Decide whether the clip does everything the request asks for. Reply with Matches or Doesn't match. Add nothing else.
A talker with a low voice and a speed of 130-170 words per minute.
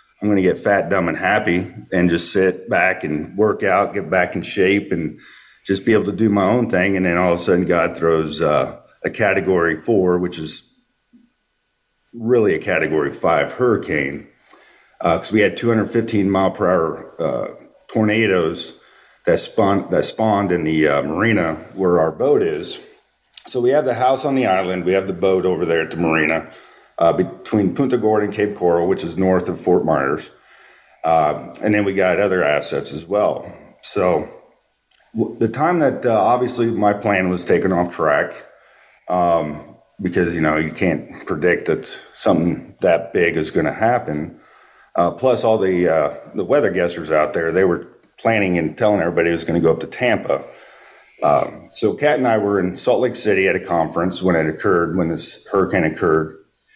Doesn't match